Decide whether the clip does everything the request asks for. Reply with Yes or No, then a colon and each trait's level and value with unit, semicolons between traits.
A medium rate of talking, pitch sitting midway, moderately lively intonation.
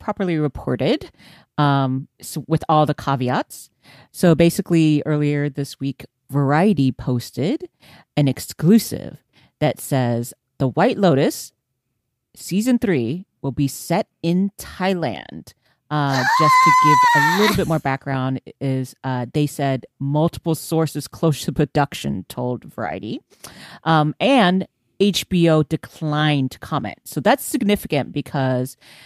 No: slow, 120 wpm; medium, 150 Hz; average, 4.6 semitones